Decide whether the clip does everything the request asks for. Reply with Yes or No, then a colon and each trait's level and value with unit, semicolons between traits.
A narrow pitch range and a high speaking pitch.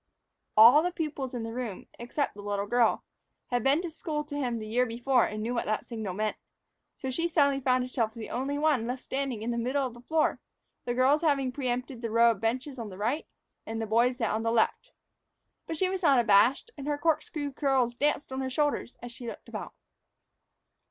No: average, 3.8 semitones; very high, 250 Hz